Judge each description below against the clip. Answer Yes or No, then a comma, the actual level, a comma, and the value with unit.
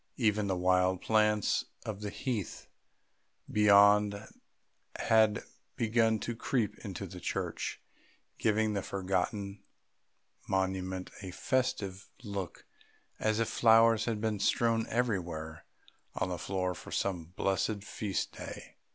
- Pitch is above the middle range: No, low, 100 Hz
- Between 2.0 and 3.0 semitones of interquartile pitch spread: Yes, average, 2.7 semitones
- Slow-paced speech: Yes, slow, 115 wpm